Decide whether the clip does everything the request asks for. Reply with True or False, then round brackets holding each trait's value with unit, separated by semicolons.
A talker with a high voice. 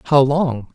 False (135 Hz)